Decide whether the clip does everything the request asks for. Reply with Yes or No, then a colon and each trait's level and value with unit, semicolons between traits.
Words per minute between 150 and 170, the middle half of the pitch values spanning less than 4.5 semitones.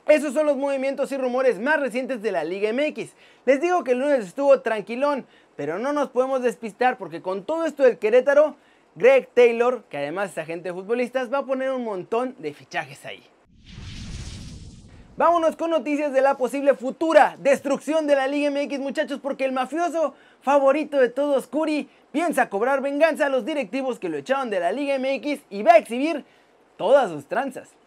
No: average, 185 wpm; average, 2.8 semitones